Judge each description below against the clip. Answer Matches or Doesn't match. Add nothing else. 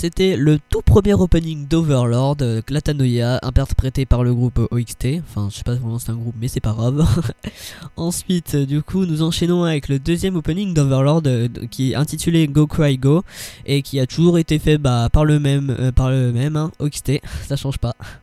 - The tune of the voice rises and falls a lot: Doesn't match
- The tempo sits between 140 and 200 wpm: Matches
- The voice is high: Doesn't match